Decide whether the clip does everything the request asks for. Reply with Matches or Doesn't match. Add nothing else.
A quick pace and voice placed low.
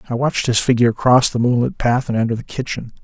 Matches